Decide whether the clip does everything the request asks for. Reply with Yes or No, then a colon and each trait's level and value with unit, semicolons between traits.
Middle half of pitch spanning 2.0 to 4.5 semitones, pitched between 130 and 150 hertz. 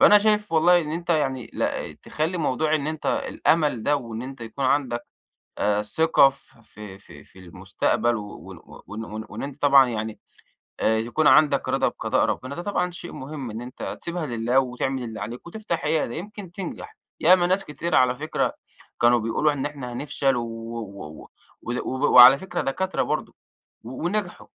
No: wide, 5.4 semitones; low, 135 Hz